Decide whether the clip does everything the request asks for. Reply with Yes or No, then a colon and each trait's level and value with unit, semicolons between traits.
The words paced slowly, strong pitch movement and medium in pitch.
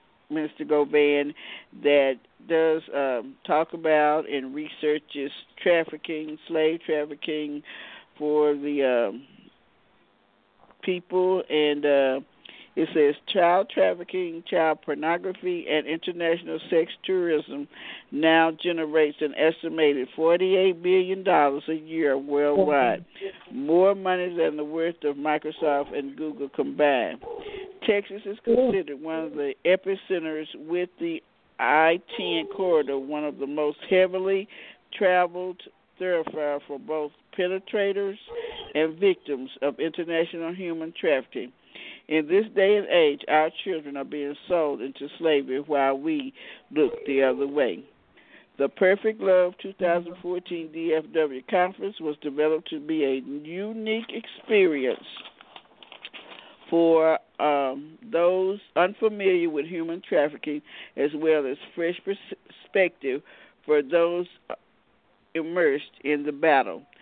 No: slow, 115 wpm; average, 3.9 semitones; medium, 160 Hz